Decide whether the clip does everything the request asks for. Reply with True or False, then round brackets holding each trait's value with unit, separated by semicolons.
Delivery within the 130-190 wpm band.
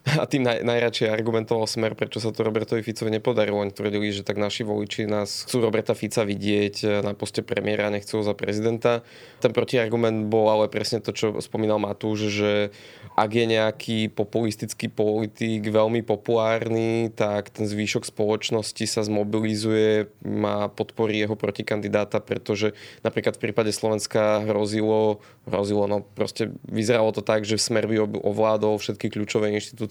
True (155 wpm)